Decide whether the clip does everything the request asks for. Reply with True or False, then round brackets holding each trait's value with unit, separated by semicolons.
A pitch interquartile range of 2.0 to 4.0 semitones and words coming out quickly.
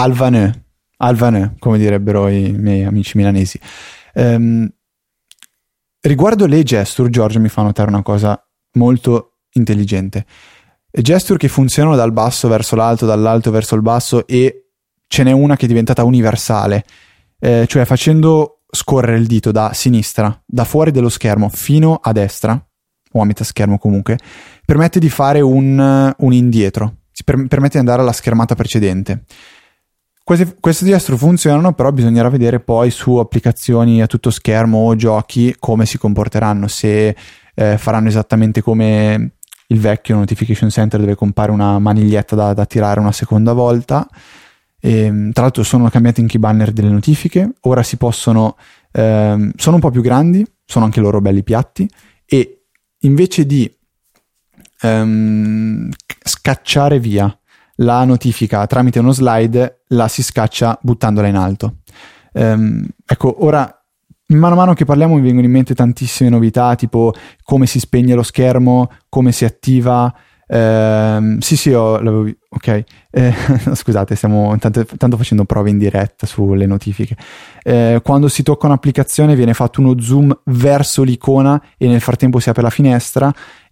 False (3.2 semitones; 150 wpm)